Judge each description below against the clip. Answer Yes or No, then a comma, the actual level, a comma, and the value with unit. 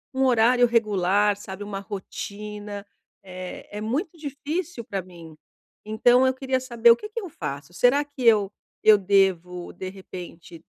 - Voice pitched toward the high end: Yes, high, 210 Hz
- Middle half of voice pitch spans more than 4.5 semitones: Yes, average, 4.9 semitones